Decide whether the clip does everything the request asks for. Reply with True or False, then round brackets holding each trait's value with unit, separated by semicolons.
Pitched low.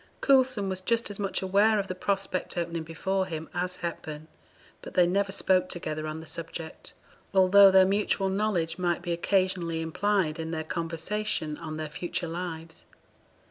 False (180 Hz)